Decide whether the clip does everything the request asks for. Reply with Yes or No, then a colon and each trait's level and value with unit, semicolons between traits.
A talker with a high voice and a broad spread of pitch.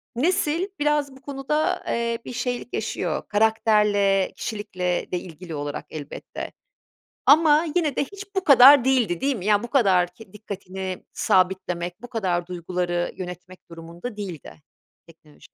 Yes: high, 205 Hz; wide, 6.8 semitones